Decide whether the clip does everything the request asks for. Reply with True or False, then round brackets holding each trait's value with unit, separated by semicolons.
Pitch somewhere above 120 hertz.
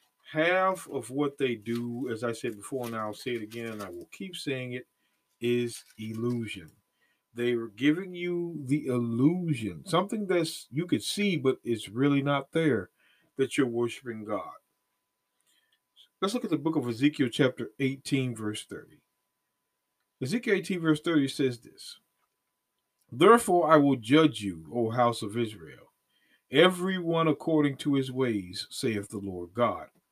True (135 Hz)